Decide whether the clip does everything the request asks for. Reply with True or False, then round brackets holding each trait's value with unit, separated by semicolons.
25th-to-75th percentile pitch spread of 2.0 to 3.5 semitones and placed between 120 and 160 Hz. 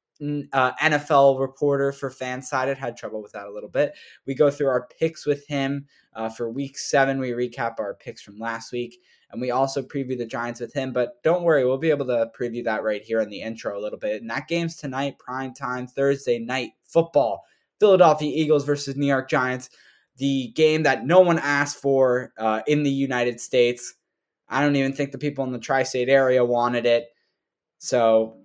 True (2.8 semitones; 135 Hz)